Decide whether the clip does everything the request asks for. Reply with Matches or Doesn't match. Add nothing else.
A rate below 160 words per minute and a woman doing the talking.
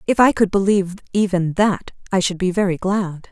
Doesn't match